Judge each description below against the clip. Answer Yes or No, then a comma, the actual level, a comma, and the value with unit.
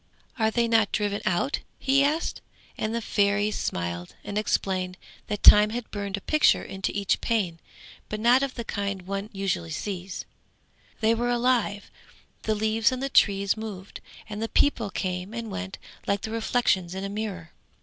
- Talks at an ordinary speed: Yes, average, 170 wpm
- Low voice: No, high, 210 Hz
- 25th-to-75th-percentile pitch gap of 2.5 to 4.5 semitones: Yes, average, 2.9 semitones